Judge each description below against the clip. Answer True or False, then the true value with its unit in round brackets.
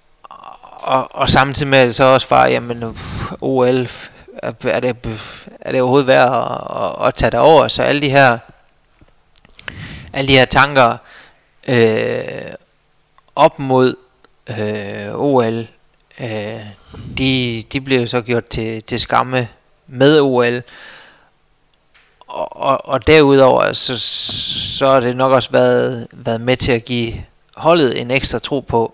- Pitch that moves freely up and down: False (2.8 semitones)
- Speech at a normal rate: False (140 wpm)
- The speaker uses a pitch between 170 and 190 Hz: False (125 Hz)